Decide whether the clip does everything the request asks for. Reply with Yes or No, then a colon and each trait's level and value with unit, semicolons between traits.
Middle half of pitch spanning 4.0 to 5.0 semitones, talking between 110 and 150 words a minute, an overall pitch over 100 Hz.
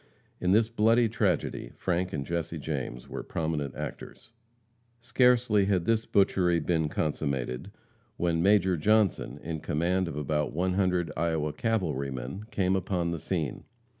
No: average, 4.5 semitones; slow, 135 wpm; very low, 85 Hz